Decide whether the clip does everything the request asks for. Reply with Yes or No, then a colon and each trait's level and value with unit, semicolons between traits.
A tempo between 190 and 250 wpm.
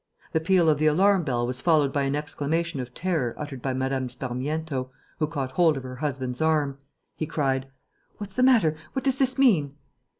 Yes: average, 195 wpm